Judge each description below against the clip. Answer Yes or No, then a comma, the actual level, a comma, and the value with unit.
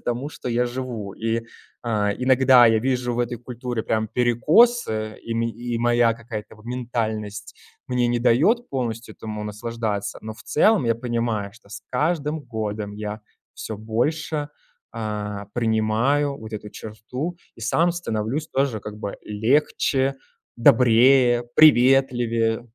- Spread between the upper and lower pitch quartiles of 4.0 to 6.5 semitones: No, average, 2.8 semitones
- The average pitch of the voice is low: Yes, low, 120 Hz